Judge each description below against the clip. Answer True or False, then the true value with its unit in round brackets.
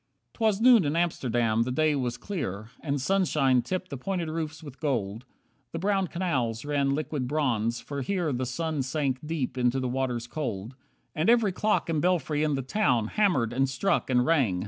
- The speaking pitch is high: False (140 Hz)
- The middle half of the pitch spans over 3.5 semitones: True (5.1 semitones)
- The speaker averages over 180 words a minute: True (190 wpm)